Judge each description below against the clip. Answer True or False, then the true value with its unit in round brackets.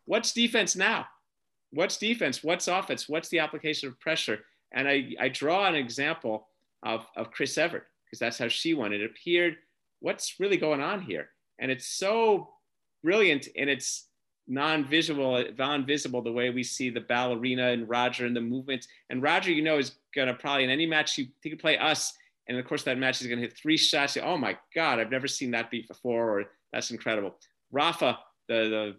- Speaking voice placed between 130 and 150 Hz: True (140 Hz)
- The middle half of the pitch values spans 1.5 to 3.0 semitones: False (4.4 semitones)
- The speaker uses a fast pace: False (195 wpm)